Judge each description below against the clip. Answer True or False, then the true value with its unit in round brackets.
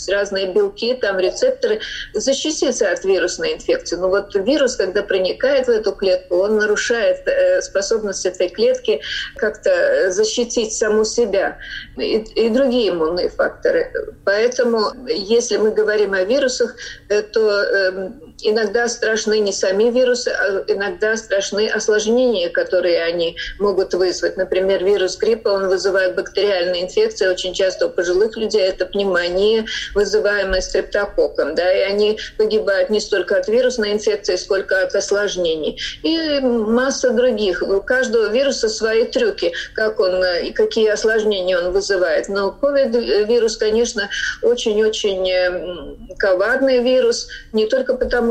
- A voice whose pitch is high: True (220 Hz)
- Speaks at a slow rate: False (125 wpm)